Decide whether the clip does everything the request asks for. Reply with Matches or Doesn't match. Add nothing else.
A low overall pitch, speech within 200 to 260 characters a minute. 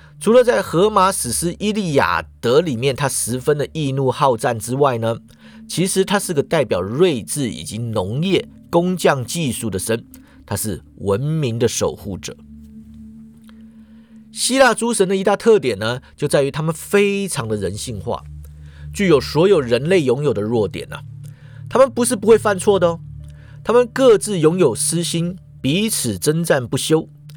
Doesn't match